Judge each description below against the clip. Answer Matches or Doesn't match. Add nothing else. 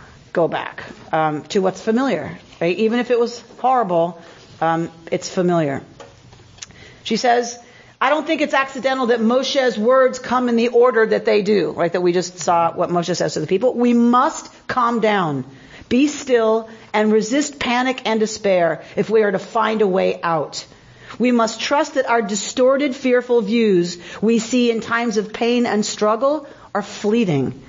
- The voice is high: Matches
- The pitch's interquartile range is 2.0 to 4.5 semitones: Doesn't match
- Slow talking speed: Doesn't match